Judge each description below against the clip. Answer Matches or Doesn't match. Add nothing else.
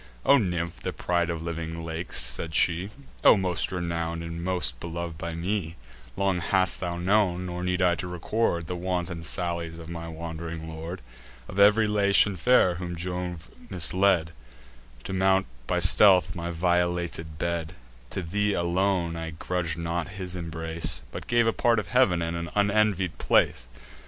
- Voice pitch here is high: Doesn't match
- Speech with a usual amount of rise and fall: Doesn't match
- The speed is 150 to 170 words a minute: Matches